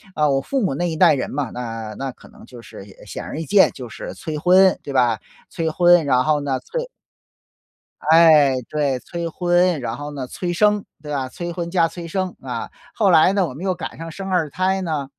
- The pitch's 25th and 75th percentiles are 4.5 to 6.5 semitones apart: Yes, average, 4.8 semitones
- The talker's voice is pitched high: No, medium, 160 Hz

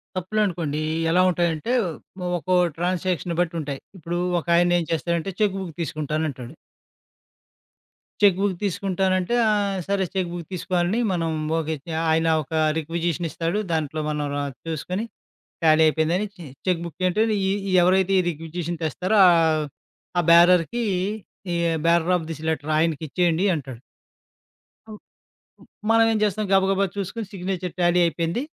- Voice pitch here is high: No, medium, 175 Hz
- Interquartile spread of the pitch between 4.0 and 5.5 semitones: No, average, 2.8 semitones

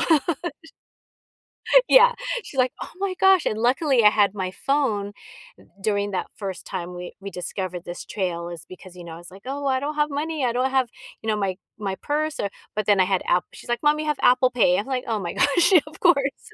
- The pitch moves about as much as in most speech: No, wide, 7.0 semitones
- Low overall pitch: No, high, 220 Hz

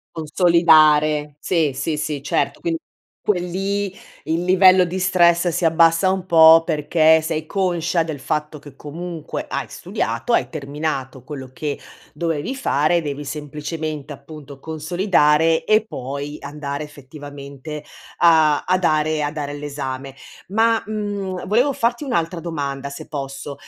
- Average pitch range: Yes, average, 3.1 semitones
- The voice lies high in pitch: No, medium, 155 Hz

